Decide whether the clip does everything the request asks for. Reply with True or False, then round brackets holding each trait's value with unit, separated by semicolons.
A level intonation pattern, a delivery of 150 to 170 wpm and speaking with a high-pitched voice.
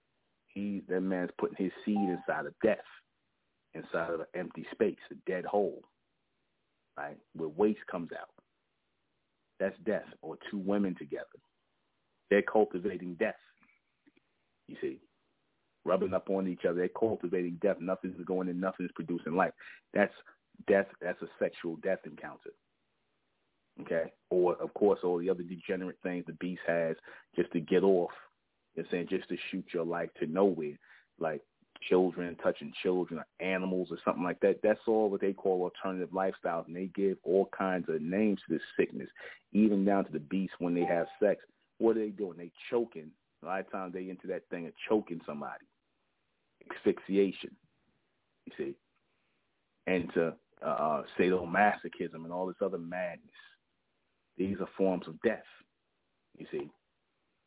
False (1.9 semitones; 160 wpm; 90 Hz)